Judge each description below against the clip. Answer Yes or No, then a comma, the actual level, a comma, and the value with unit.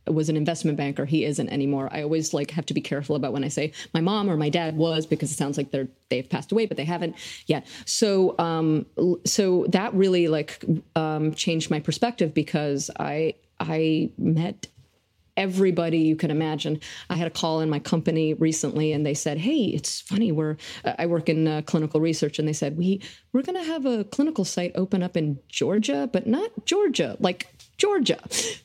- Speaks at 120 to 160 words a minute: No, average, 200 wpm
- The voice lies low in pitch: No, medium, 160 Hz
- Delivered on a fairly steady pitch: No, average, 3.1 semitones